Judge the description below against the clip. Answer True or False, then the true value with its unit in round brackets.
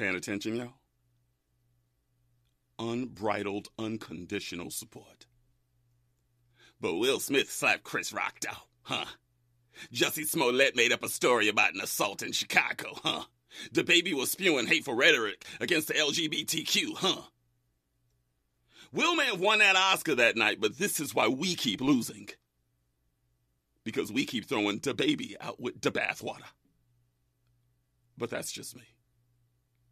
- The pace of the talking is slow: True (130 wpm)